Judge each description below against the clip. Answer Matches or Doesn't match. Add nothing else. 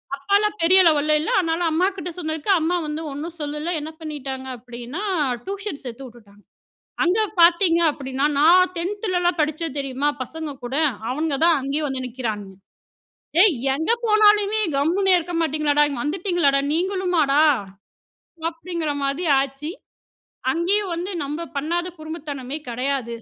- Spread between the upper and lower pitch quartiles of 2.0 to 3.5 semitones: Doesn't match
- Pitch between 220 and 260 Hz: Doesn't match